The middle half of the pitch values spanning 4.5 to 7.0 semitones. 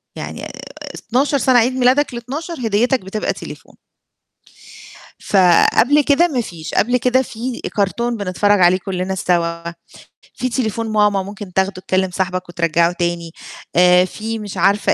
Yes: average, 5.1 semitones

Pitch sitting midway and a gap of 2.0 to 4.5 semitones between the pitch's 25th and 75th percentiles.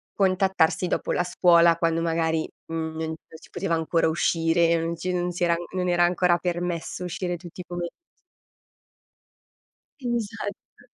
No: medium, 175 Hz; narrow, 1.5 semitones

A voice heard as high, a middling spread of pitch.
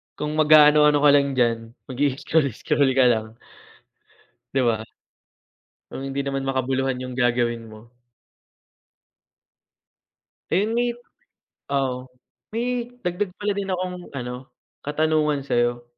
No: medium, 140 Hz; average, 3.8 semitones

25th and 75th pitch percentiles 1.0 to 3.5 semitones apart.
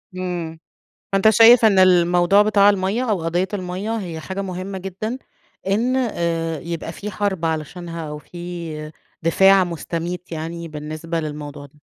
Yes: average, 3.1 semitones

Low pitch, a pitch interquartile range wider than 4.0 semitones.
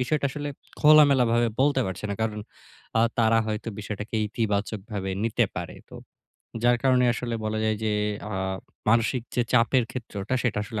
No: low, 115 Hz; average, 2.9 semitones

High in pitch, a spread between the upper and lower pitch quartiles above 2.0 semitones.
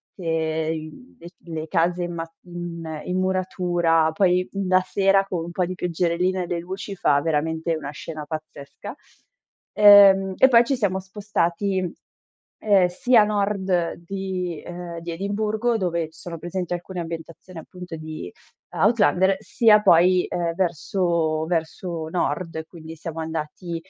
No: medium, 175 Hz; narrow, 2.6 semitones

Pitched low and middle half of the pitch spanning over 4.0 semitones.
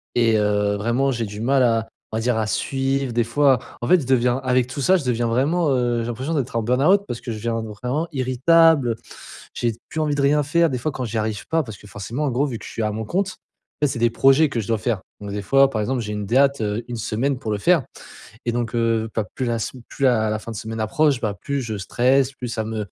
No: low, 120 Hz; average, 3.5 semitones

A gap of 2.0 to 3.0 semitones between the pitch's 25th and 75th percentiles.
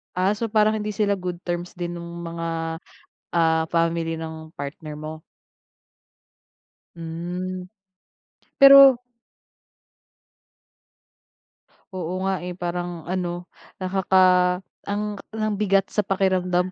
Yes: narrow, 2.6 semitones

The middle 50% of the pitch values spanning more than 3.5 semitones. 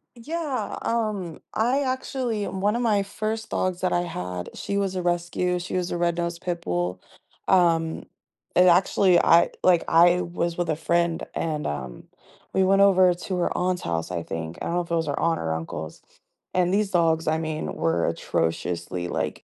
No: average, 3.1 semitones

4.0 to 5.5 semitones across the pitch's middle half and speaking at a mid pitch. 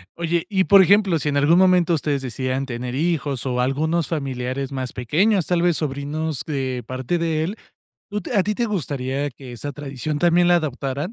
Yes: average, 4.6 semitones; medium, 150 Hz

